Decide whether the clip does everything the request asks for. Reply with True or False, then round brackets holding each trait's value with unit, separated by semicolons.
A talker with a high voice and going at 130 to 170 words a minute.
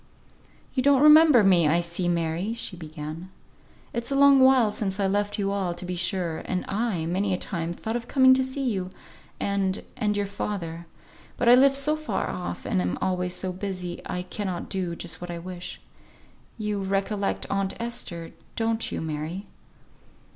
False (195 Hz; 180 wpm)